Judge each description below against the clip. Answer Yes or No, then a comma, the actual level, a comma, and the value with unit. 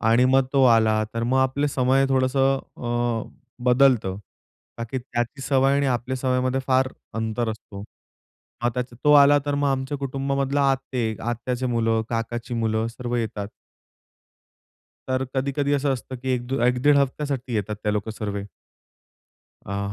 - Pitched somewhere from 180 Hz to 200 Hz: No, low, 125 Hz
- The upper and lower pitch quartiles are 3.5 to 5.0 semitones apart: No, average, 2.7 semitones